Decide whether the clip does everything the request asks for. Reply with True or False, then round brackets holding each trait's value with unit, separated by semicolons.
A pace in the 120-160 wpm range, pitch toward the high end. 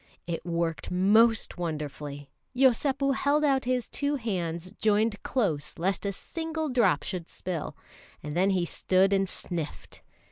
True (140 wpm; 195 Hz)